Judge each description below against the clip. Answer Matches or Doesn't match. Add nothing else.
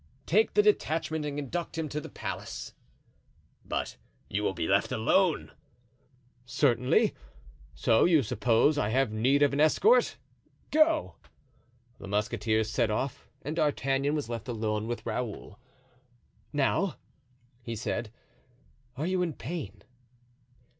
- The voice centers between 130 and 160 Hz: Matches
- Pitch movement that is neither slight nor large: Doesn't match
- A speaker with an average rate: Doesn't match